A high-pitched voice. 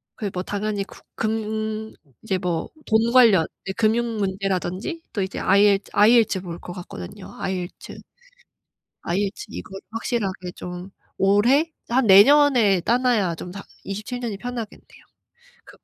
Yes: high, 205 Hz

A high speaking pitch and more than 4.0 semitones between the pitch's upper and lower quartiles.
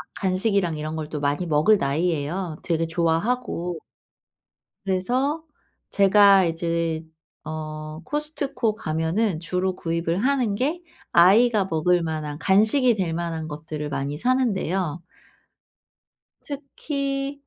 No: medium, 180 Hz; wide, 5.6 semitones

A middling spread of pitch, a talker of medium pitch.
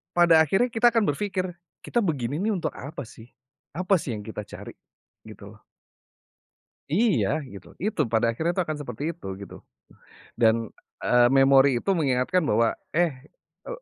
No: wide, 7.4 semitones; medium, 155 Hz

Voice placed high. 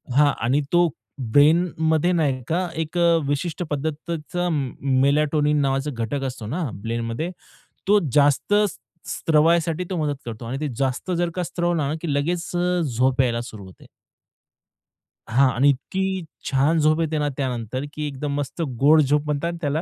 No: medium, 150 Hz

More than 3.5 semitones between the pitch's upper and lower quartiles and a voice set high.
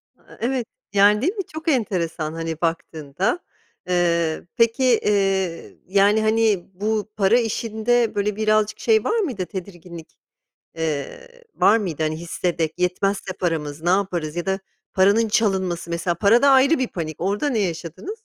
Yes: average, 4.8 semitones; high, 195 Hz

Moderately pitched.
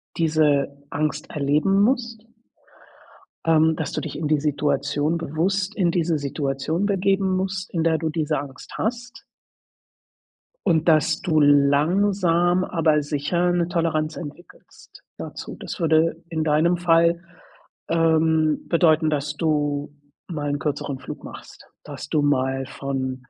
Yes: medium, 160 Hz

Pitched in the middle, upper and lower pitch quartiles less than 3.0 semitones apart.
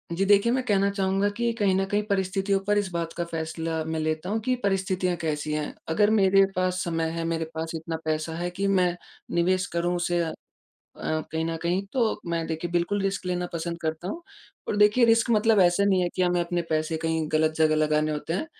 No: medium, 175 Hz; average, 3.4 semitones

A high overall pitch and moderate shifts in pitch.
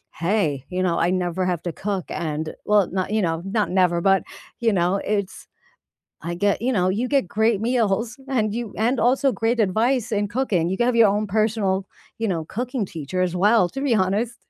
Yes: high, 200 Hz; average, 3.9 semitones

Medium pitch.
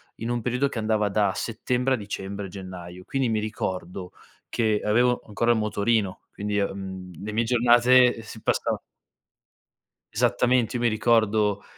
No: low, 110 Hz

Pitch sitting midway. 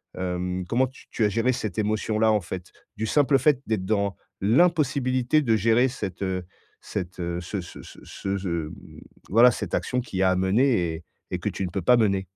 No: low, 105 Hz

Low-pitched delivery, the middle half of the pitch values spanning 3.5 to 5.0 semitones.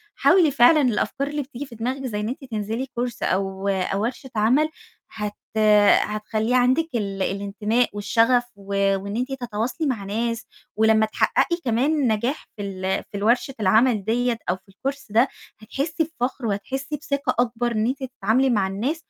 No: high, 230 Hz; average, 4.0 semitones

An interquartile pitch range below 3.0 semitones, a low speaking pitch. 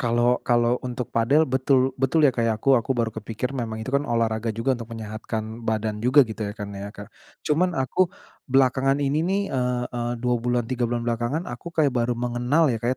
Yes: narrow, 2.6 semitones; low, 120 Hz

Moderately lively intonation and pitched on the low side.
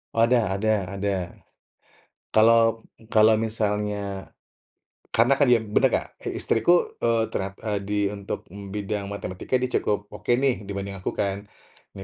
No: narrow, 2.2 semitones; low, 105 Hz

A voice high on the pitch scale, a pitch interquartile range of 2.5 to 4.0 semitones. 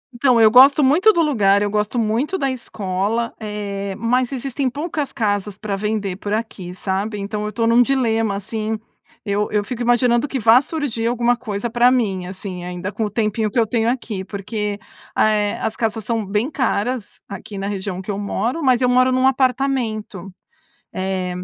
Yes: high, 220 Hz; average, 3.6 semitones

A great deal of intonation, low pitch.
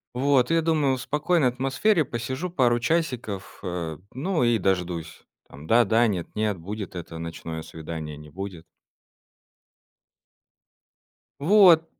Yes: wide, 8.6 semitones; low, 120 Hz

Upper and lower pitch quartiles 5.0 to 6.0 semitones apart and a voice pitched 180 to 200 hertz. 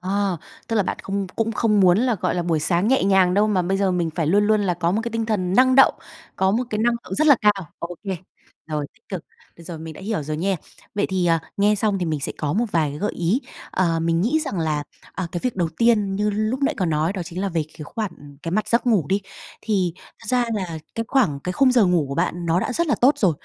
No: average, 4.3 semitones; high, 190 Hz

